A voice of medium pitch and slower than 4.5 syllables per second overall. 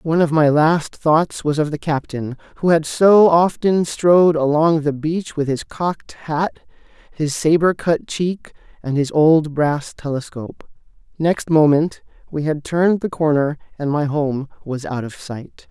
Yes: medium, 155 Hz; 4.3 syllables/s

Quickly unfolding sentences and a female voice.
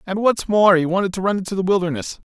No: fast, 260 wpm; male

